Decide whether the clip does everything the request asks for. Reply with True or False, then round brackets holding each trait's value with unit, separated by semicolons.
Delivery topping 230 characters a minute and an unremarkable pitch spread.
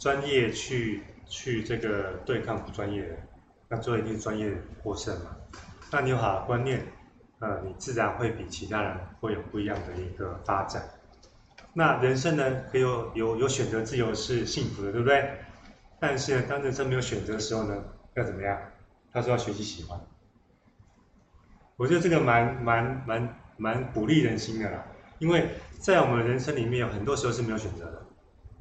True (265 characters per minute; 3.8 semitones)